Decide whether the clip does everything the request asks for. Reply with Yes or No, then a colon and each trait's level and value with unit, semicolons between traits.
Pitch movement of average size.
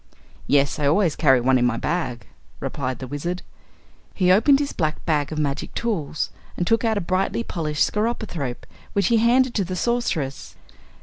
No: wide, 7.3 semitones